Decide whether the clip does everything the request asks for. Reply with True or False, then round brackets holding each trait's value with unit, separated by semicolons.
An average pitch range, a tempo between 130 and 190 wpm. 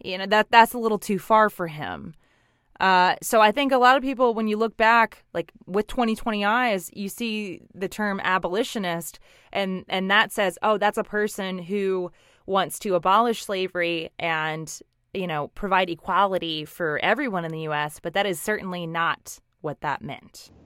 True (3.6 semitones; 180 wpm)